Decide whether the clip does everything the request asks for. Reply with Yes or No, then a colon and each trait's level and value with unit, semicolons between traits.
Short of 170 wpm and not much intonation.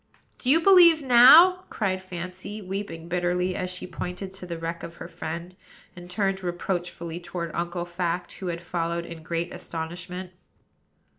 Yes: average, 155 wpm; narrow, 2.0 semitones